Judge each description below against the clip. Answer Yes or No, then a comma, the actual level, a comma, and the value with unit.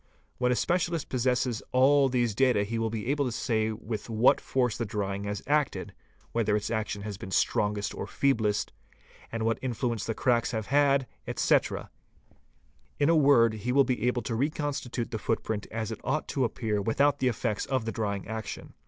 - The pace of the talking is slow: No, average, 190 wpm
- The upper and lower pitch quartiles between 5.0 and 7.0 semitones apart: No, average, 3.4 semitones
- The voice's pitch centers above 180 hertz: No, low, 115 Hz